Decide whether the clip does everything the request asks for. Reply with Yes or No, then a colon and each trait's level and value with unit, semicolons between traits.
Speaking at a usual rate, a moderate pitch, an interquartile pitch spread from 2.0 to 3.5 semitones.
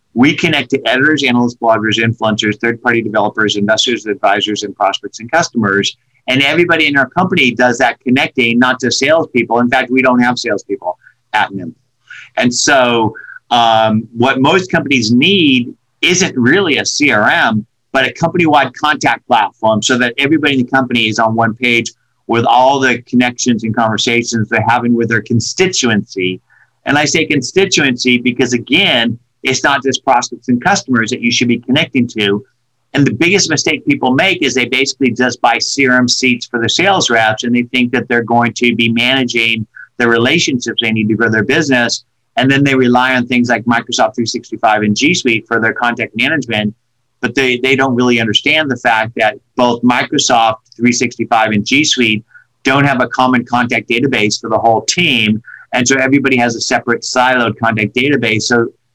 No: average, 175 wpm; low, 120 Hz; narrow, 2.5 semitones